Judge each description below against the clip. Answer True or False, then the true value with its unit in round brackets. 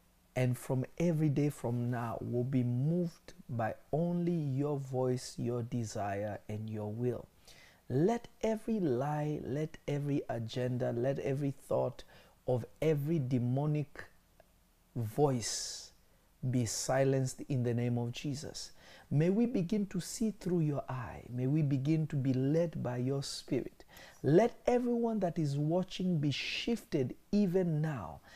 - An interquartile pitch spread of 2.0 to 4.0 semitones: False (5.1 semitones)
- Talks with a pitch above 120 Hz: True (140 Hz)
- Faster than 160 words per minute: False (135 wpm)